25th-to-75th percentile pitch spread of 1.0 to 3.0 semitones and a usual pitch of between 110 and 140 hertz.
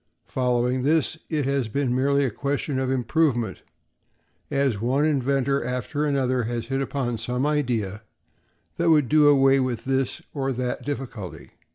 Yes: narrow, 2.4 semitones; low, 135 Hz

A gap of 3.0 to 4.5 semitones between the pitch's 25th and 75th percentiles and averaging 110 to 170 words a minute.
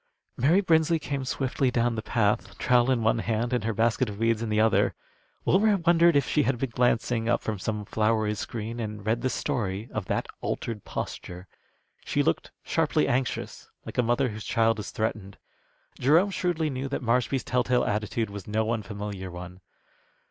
No: average, 3.5 semitones; average, 180 wpm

